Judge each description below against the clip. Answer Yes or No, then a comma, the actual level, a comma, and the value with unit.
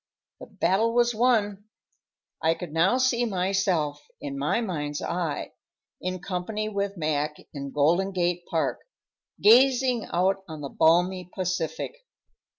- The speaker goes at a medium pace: No, slow, 130 wpm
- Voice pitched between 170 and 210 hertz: Yes, medium, 185 Hz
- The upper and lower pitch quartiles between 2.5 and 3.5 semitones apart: No, average, 4.8 semitones